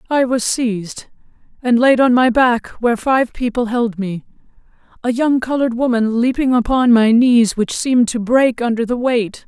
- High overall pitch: Yes, high, 240 Hz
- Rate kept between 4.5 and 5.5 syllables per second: Yes, 4.8 syllables/s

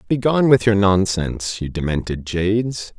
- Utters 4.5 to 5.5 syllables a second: Yes, 5.0 syllables/s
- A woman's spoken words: No, male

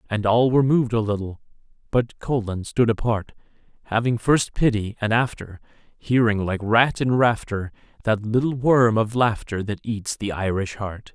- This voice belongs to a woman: No, male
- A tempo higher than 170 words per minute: No, average, 160 wpm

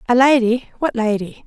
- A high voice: Yes, high, 235 Hz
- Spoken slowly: Yes, slow, 125 wpm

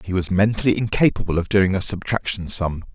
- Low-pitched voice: Yes, very low, 95 Hz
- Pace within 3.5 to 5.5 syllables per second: No, 5.7 syllables/s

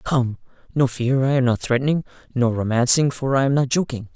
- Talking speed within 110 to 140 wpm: No, average, 200 wpm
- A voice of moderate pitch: No, low, 130 Hz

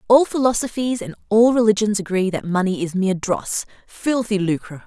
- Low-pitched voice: No, high, 205 Hz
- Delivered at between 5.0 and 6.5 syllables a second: Yes, 5.3 syllables/s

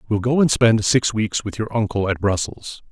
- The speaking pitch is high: No, low, 110 Hz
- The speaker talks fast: Yes, fast, 225 wpm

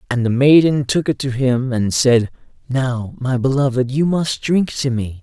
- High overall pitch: No, low, 130 Hz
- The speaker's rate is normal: Yes, average, 195 wpm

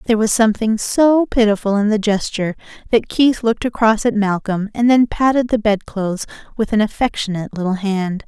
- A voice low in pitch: No, high, 215 Hz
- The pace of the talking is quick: No, average, 175 wpm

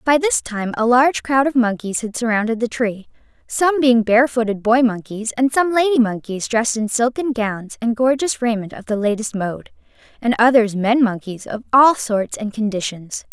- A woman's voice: Yes, female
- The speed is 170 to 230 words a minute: Yes, average, 185 wpm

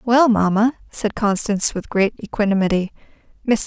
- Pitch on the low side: No, high, 215 Hz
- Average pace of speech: No, slow, 115 wpm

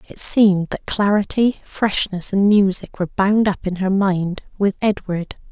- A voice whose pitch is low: No, high, 195 Hz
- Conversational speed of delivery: Yes, average, 165 wpm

